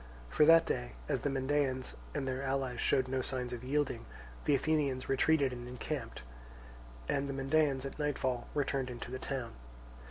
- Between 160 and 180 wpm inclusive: Yes, average, 165 wpm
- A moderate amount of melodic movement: No, narrow, 2.1 semitones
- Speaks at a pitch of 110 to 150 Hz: Yes, low, 135 Hz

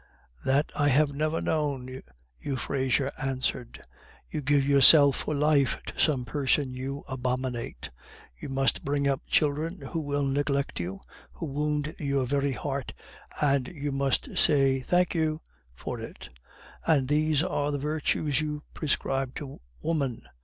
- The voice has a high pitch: No, medium, 140 Hz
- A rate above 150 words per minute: No, average, 140 wpm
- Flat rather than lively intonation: Yes, narrow, 2.0 semitones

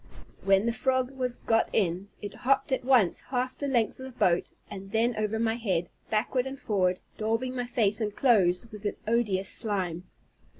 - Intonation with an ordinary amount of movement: Yes, average, 4.2 semitones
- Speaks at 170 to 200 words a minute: Yes, average, 185 wpm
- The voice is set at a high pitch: Yes, high, 225 Hz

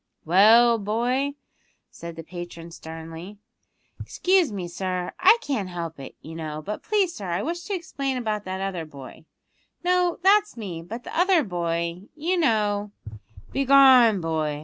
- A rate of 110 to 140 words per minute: No, average, 160 wpm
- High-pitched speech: Yes, high, 205 Hz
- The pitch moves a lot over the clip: Yes, wide, 8.5 semitones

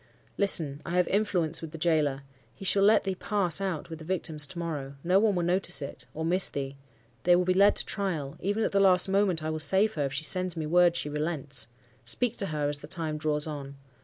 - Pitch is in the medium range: Yes, medium, 170 Hz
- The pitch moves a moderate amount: Yes, average, 4.1 semitones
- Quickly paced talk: Yes, fast, 235 wpm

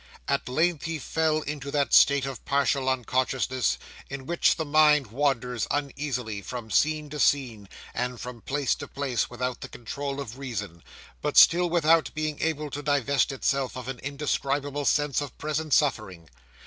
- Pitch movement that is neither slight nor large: Yes, average, 3.0 semitones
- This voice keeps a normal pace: Yes, average, 160 wpm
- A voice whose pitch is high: No, medium, 140 Hz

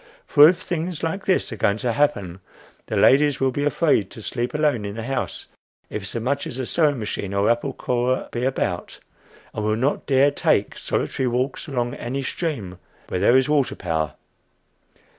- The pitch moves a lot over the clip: No, average, 4.8 semitones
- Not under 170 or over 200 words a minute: Yes, average, 190 wpm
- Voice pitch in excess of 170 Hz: No, low, 130 Hz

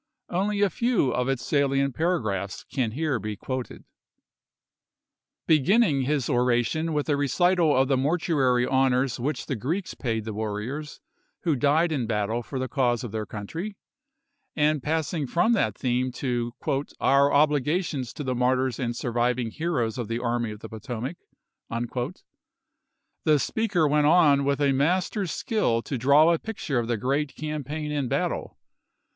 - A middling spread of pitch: Yes, average, 4.3 semitones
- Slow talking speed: No, average, 165 wpm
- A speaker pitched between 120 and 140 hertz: Yes, low, 135 Hz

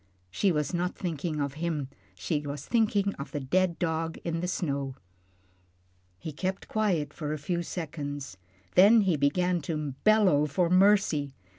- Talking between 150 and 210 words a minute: Yes, average, 160 wpm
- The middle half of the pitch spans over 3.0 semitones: Yes, average, 4.1 semitones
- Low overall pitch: No, medium, 165 Hz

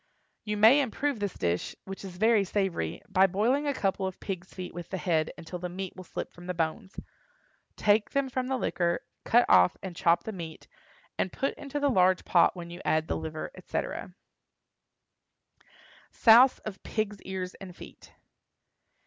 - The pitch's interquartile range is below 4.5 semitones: Yes, average, 4.0 semitones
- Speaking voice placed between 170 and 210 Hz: Yes, high, 190 Hz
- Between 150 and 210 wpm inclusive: Yes, average, 175 wpm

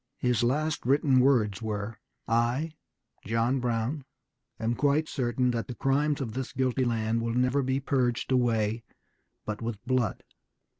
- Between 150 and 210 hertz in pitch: No, low, 125 Hz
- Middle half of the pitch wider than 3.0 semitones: No, average, 2.7 semitones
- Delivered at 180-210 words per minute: No, average, 145 wpm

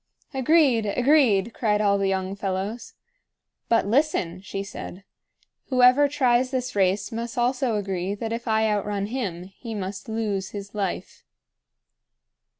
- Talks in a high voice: Yes, high, 215 Hz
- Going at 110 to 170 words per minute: Yes, slow, 135 wpm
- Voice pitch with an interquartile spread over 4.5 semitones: No, average, 4.0 semitones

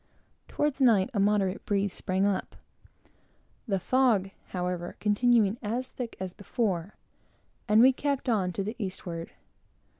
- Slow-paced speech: Yes, slow, 130 wpm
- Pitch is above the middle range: Yes, high, 205 Hz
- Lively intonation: No, average, 4.2 semitones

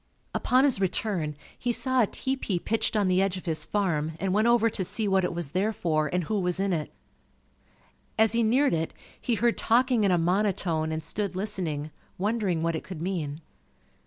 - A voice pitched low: No, high, 190 Hz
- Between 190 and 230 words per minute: Yes, average, 200 wpm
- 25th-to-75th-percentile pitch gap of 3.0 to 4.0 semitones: No, average, 4.7 semitones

